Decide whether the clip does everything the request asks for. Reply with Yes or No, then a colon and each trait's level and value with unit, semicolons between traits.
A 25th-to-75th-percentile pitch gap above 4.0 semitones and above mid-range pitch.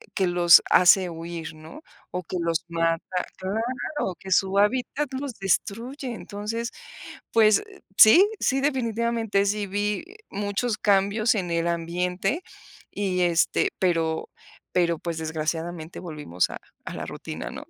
Yes: average, 5.0 semitones; high, 195 Hz